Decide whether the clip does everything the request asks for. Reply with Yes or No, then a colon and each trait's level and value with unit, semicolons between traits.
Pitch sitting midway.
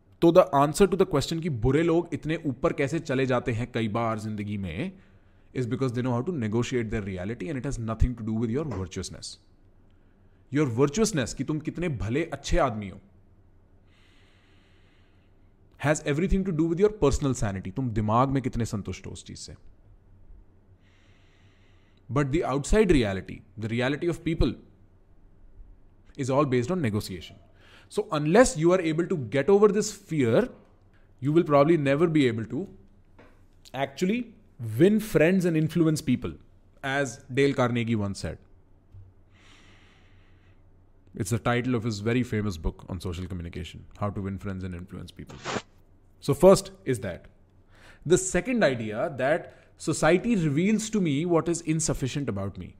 No: low, 115 Hz